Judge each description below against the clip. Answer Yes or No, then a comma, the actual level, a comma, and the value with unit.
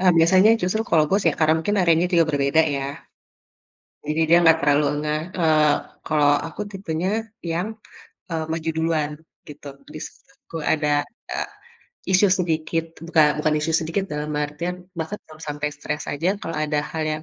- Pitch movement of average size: No, narrow, 2.0 semitones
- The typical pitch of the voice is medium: Yes, medium, 160 Hz